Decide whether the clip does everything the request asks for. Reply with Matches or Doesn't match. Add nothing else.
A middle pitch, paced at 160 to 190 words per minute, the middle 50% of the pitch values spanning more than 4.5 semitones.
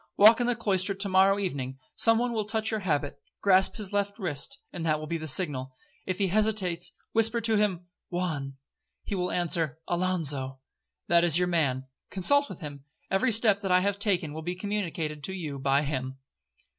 Matches